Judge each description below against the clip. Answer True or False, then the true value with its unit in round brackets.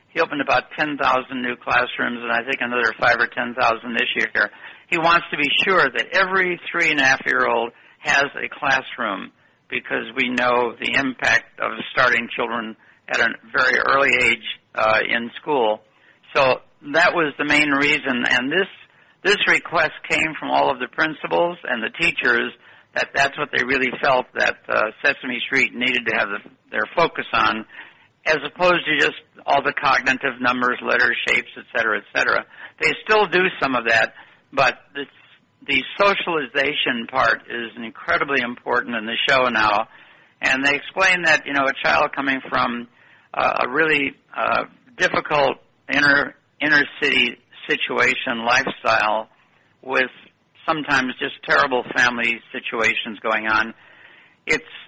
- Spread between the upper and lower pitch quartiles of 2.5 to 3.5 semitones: False (4.1 semitones)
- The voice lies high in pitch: False (135 Hz)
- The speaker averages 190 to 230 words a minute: False (155 wpm)